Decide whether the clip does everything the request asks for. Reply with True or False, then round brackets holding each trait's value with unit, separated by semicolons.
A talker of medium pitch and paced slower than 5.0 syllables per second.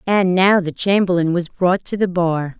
True (180 Hz; 4.5 syllables/s)